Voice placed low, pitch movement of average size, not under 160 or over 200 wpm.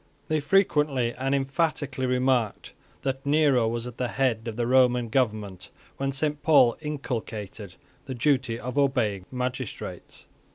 No: low, 130 Hz; average, 3.0 semitones; slow, 135 wpm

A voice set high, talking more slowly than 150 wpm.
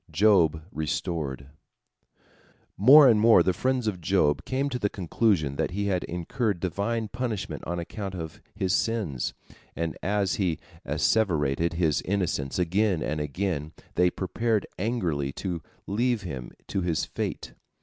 No: very low, 95 Hz; average, 140 wpm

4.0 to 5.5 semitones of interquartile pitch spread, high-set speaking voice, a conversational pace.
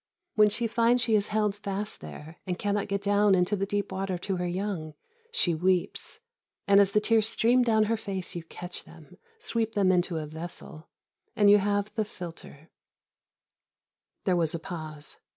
No: average, 3.2 semitones; high, 200 Hz; average, 180 wpm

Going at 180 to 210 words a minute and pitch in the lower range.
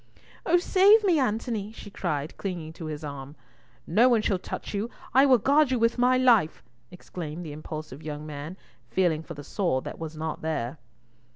No: average, 185 wpm; medium, 180 Hz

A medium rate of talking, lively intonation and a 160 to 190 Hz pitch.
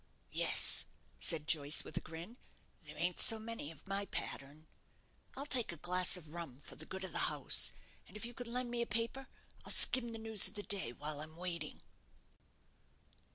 Yes: average, 195 wpm; wide, 6.5 semitones; medium, 185 Hz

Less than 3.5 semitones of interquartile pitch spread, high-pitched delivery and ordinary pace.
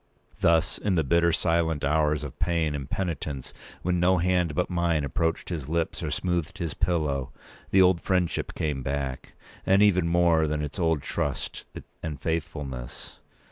No: average, 2.9 semitones; very low, 80 Hz; average, 160 wpm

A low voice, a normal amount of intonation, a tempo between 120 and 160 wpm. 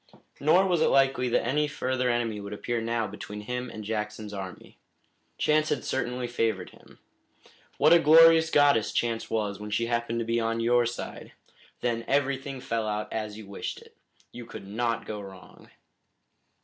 No: low, 115 Hz; average, 3.7 semitones; average, 175 wpm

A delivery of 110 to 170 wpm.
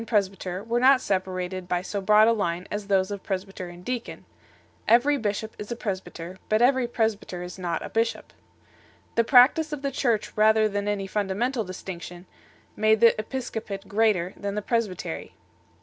No: average, 180 wpm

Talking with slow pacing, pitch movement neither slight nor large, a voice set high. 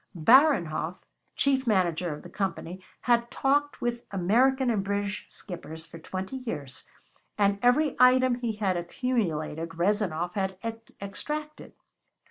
No: slow, 120 wpm; wide, 6.4 semitones; high, 200 Hz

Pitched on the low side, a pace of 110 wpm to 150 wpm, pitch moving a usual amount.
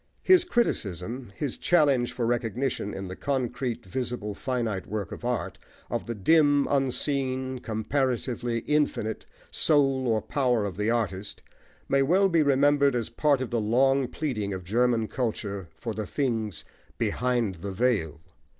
Yes: low, 120 Hz; average, 145 wpm; average, 4.1 semitones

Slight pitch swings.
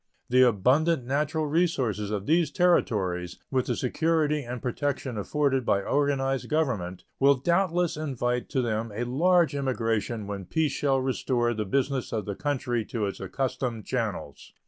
No: average, 4.6 semitones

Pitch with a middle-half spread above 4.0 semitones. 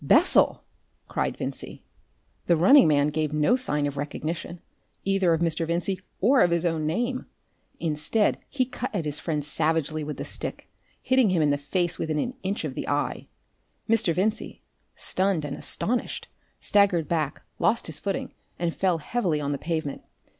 Yes: average, 4.5 semitones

